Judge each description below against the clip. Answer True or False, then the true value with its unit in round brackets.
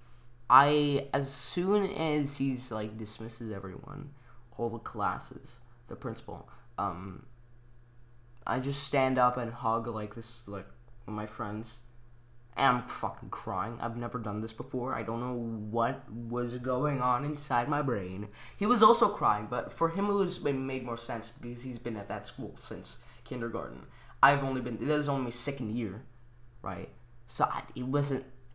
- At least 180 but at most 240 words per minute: False (170 wpm)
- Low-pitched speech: True (120 Hz)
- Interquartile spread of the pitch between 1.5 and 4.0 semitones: True (2.7 semitones)